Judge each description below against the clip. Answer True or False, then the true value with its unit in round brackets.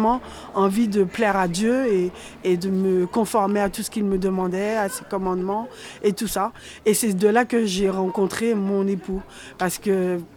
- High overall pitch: True (200 Hz)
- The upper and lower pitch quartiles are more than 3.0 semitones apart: False (2.4 semitones)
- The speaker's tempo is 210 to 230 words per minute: False (190 wpm)